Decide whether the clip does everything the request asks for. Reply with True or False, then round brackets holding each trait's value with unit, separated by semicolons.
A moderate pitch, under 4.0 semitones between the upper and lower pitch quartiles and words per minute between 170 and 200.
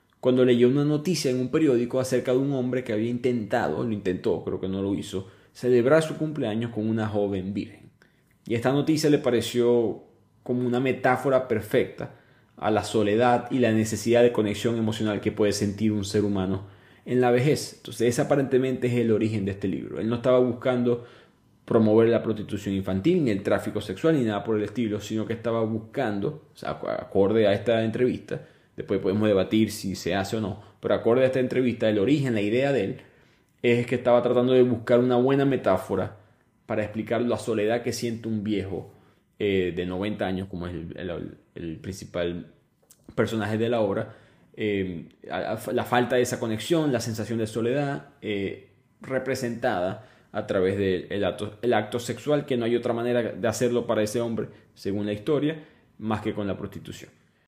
False (115 Hz; 3.1 semitones; 185 wpm)